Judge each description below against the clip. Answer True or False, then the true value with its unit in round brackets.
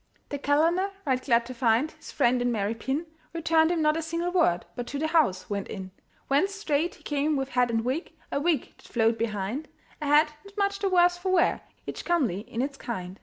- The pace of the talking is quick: True (220 wpm)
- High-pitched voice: True (285 Hz)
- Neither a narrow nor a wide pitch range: False (6.0 semitones)